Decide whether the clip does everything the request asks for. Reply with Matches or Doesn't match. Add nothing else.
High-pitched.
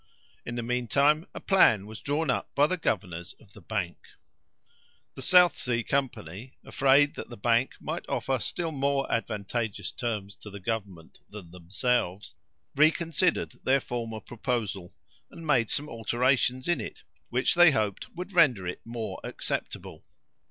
Doesn't match